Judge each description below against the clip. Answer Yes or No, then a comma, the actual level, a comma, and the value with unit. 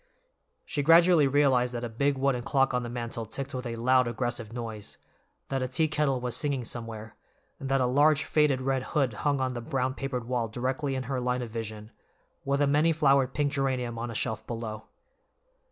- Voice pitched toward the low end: Yes, low, 130 Hz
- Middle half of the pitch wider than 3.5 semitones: No, average, 2.7 semitones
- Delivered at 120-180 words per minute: No, average, 200 wpm